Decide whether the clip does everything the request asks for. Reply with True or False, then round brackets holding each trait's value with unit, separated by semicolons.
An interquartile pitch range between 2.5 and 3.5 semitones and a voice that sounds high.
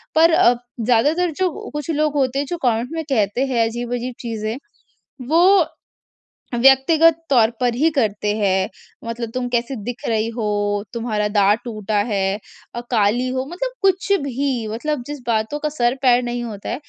False (4.6 semitones; 245 Hz)